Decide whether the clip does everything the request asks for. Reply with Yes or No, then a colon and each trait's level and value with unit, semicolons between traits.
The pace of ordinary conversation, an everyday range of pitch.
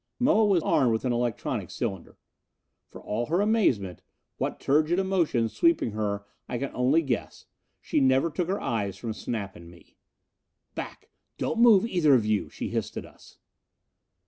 No: average, 170 wpm; wide, 8.7 semitones